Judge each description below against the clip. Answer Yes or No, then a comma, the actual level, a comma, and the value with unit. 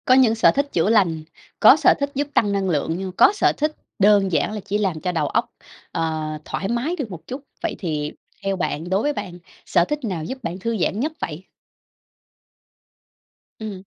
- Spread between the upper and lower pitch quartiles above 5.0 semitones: Yes, wide, 5.6 semitones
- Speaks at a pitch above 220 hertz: No, high, 195 Hz